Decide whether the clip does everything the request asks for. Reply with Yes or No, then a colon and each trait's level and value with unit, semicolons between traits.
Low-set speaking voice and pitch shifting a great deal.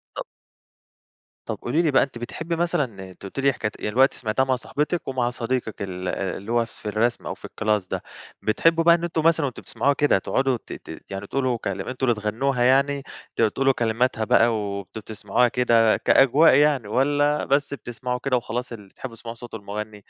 No: low, 120 Hz; average, 4.1 semitones